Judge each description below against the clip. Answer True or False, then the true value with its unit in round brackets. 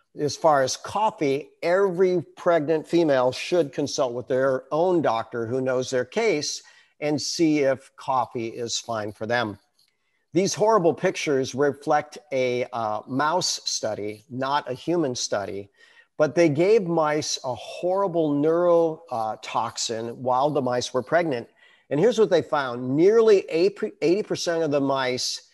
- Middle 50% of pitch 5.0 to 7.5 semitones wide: True (5.4 semitones)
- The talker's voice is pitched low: False (150 Hz)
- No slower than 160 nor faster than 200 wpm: False (140 wpm)